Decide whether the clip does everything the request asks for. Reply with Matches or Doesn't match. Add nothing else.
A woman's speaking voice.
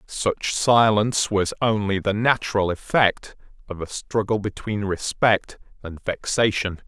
Doesn't match